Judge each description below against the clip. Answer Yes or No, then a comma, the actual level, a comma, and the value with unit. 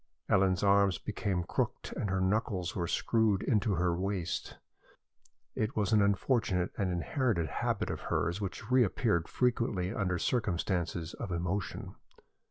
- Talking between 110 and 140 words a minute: Yes, slow, 135 wpm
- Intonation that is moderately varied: Yes, average, 3.3 semitones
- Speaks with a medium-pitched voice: No, very low, 95 Hz